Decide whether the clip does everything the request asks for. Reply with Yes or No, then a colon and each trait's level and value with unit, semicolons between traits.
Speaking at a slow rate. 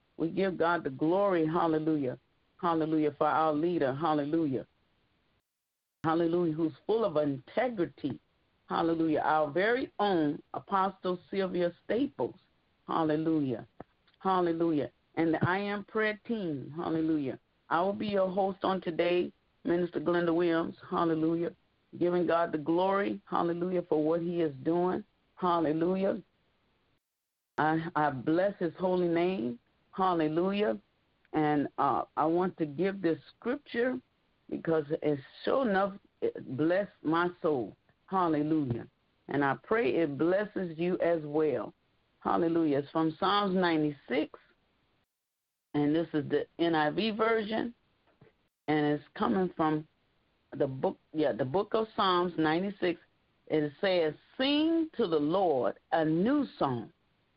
Yes: slow, 125 wpm